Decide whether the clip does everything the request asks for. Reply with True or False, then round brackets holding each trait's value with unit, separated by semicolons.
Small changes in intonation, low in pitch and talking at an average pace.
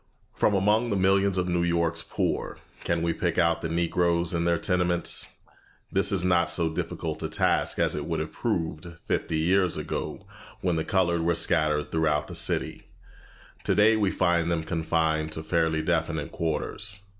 True (2.1 semitones; 85 Hz; 170 wpm)